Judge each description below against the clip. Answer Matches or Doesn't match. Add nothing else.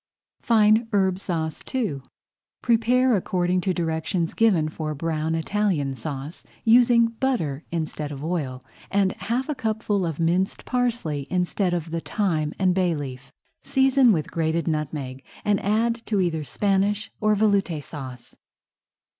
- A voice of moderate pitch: Matches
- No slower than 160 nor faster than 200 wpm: Doesn't match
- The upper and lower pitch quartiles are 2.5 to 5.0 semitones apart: Doesn't match